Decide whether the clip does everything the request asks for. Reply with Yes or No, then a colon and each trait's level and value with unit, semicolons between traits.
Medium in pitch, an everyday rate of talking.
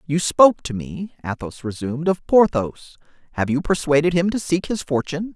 Yes: medium, 155 Hz; average, 180 wpm